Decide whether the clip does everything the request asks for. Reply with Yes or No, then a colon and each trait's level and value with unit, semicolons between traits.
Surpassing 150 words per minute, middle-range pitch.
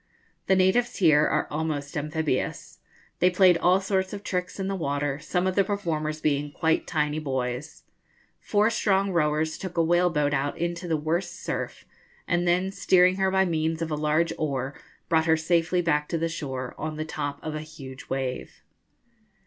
Yes: average, 180 wpm; medium, 160 Hz